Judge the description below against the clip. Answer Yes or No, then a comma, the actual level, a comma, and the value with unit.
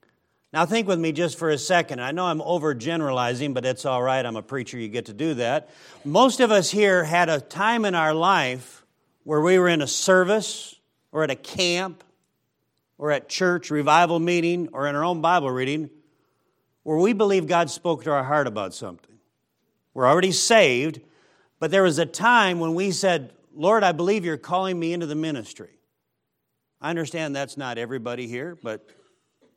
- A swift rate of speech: No, average, 185 wpm